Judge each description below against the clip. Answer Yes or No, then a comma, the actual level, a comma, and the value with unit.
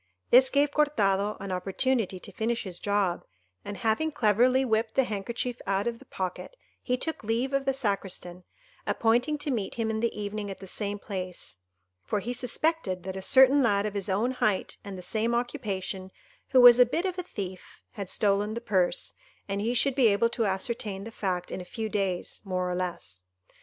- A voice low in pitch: No, high, 215 Hz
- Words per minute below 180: No, average, 200 wpm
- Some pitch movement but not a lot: Yes, average, 4.2 semitones